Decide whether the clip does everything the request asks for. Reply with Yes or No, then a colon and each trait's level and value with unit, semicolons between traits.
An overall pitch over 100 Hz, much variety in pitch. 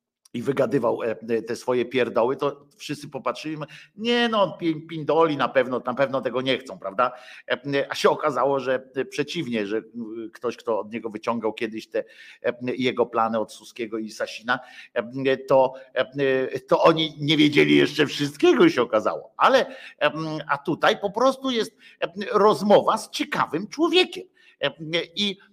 Yes: medium, 140 Hz; wide, 7.4 semitones